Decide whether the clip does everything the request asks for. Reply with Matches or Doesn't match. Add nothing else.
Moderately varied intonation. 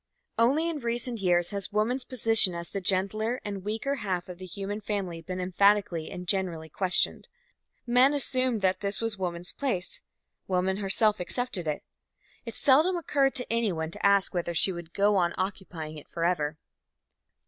Matches